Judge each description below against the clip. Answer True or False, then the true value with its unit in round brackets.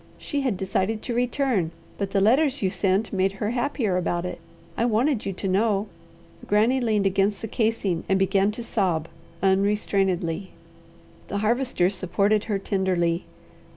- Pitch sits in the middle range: False (200 Hz)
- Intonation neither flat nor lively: True (3.0 semitones)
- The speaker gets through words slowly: False (155 wpm)